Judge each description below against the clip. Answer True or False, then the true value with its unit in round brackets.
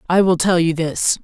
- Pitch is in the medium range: True (170 Hz)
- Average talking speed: False (245 wpm)